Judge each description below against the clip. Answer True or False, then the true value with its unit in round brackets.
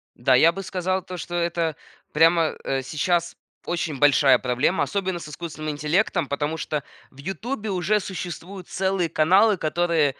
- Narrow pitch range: False (3.6 semitones)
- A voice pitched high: False (170 Hz)